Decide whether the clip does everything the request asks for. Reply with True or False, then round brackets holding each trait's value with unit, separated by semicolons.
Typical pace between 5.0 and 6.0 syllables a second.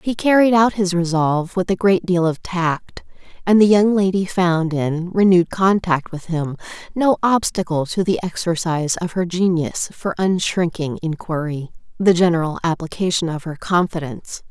False (4.8 syllables/s)